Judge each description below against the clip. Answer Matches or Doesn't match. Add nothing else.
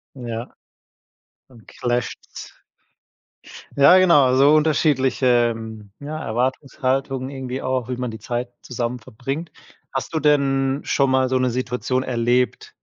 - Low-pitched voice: Matches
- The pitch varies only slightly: Matches